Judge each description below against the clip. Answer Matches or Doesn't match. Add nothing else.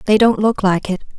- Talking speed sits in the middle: Doesn't match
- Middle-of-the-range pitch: Doesn't match